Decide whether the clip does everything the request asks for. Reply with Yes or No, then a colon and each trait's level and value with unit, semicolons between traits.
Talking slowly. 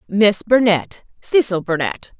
Yes: slow, 80 wpm